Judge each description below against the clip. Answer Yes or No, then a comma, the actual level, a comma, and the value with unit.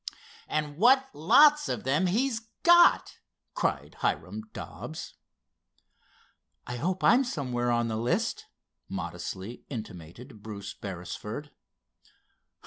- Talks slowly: Yes, slow, 100 wpm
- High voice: No, medium, 145 Hz